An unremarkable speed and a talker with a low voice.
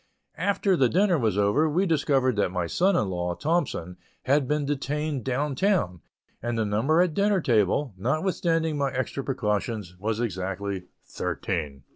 Yes: average, 155 wpm; low, 130 Hz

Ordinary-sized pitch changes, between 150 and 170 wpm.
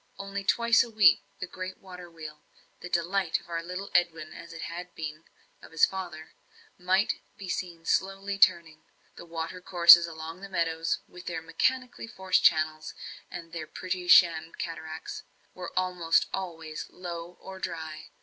No: narrow, 2.3 semitones; average, 165 wpm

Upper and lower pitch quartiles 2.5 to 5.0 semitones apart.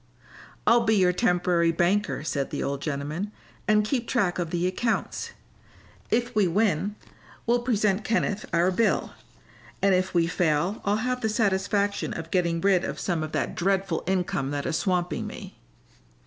Yes: average, 3.8 semitones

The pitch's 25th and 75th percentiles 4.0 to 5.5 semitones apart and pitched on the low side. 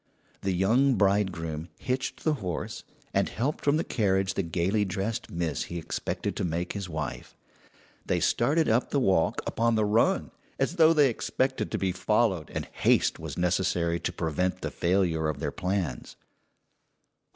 Yes: average, 5.2 semitones; very low, 95 Hz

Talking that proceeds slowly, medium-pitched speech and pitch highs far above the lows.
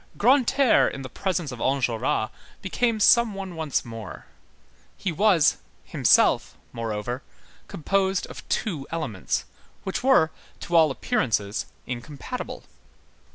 Yes: slow, 110 wpm; medium, 160 Hz; wide, 8.0 semitones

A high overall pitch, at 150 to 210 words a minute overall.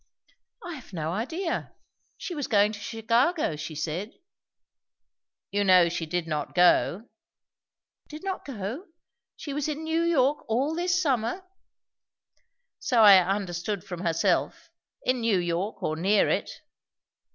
No: high, 215 Hz; average, 140 wpm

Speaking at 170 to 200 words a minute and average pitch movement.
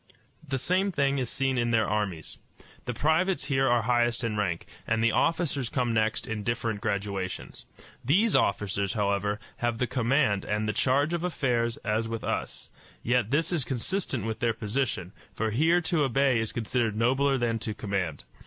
Yes: average, 175 wpm; average, 4.2 semitones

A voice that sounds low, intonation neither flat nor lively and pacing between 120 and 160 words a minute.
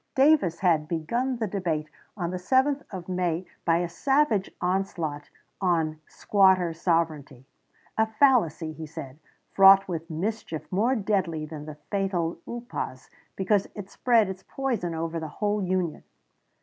No: medium, 185 Hz; average, 4.3 semitones; average, 140 wpm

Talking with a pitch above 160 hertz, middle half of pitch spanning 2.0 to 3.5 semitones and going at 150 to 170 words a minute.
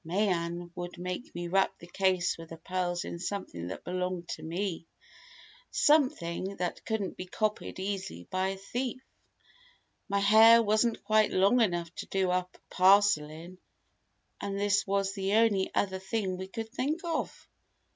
Yes: high, 190 Hz; average, 2.8 semitones; average, 160 wpm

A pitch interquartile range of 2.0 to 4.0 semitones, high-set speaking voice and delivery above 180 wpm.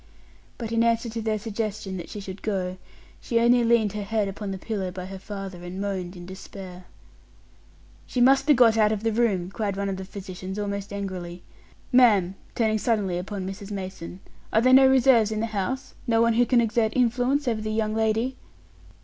Yes: average, 3.2 semitones; high, 210 Hz; average, 200 wpm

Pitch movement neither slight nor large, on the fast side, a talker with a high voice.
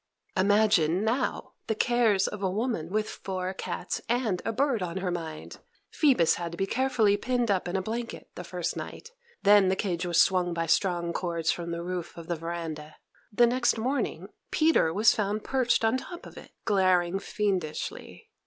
No: average, 4.6 semitones; average, 180 wpm; high, 195 Hz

